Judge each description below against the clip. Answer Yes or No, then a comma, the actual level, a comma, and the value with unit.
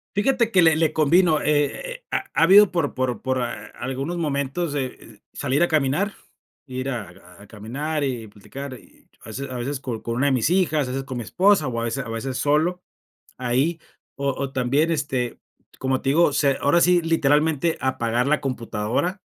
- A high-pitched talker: No, medium, 140 Hz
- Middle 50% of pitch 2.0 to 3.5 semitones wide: No, average, 4.2 semitones